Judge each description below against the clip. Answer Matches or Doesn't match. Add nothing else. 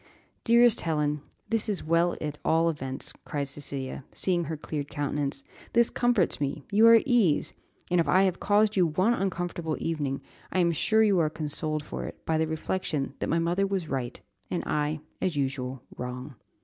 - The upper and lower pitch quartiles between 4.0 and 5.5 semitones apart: Matches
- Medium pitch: Matches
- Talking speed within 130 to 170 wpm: Doesn't match